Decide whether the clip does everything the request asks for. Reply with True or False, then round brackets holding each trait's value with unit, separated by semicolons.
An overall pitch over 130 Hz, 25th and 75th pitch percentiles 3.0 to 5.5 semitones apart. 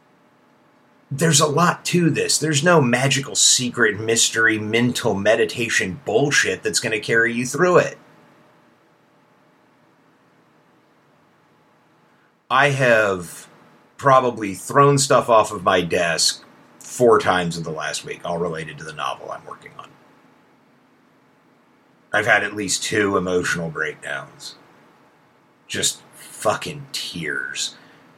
False (125 Hz; 4.7 semitones)